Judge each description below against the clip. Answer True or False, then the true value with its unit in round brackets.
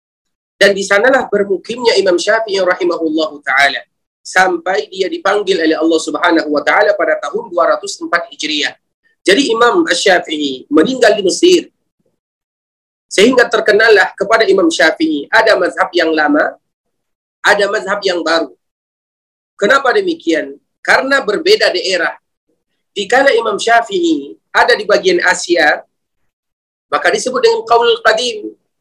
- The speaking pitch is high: True (200 Hz)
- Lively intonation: True (7.0 semitones)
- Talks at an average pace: True (115 wpm)